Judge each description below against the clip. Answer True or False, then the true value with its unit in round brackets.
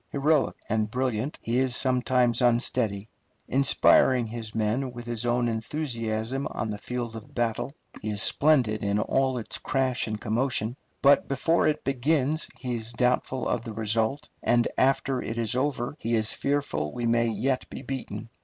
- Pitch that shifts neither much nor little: True (3.0 semitones)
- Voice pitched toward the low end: True (120 Hz)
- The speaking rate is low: False (165 wpm)